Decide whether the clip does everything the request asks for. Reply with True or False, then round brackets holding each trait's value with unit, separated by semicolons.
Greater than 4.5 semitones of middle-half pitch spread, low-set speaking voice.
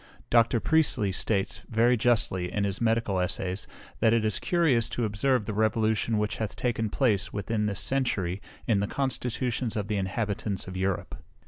False (2.9 semitones; 110 Hz)